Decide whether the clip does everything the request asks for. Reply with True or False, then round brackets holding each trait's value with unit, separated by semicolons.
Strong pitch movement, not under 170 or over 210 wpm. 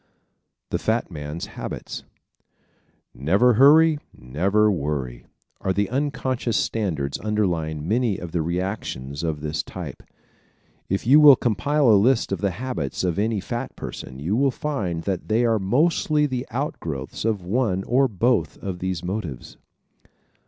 False (6.8 semitones; 150 wpm)